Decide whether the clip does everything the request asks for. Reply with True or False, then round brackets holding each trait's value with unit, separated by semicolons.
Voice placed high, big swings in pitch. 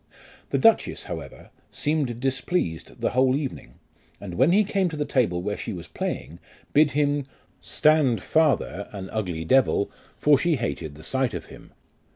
False (130 Hz; 6.9 semitones)